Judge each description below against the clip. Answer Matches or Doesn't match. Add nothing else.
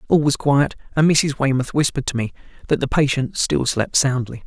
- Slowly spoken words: Doesn't match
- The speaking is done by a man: Matches